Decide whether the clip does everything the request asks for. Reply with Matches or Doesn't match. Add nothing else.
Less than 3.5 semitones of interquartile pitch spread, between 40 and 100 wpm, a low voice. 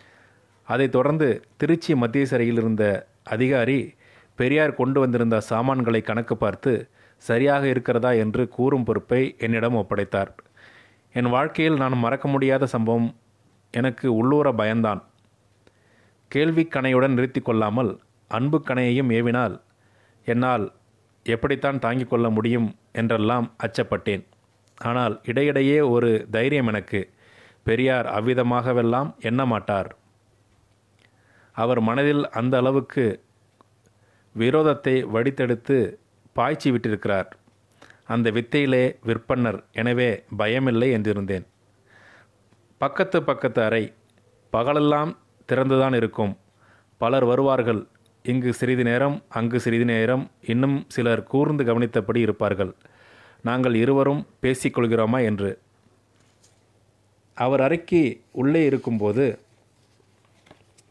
Matches